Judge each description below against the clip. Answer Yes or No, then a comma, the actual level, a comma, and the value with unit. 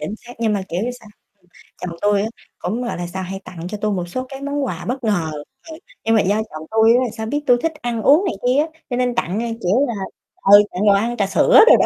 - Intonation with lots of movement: No, average, 4.4 semitones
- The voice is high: Yes, high, 220 Hz